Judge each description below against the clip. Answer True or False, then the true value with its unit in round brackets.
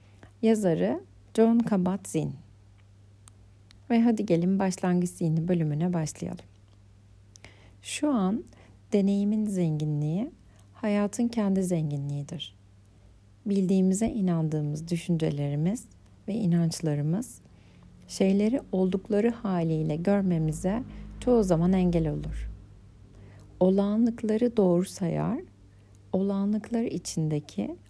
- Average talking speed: False (75 wpm)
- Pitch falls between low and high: True (165 Hz)